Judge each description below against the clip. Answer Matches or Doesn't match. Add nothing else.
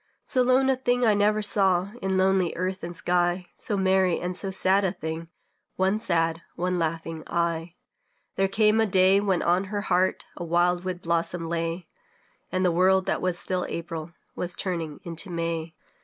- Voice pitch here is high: Doesn't match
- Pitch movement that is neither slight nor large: Doesn't match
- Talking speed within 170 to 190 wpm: Matches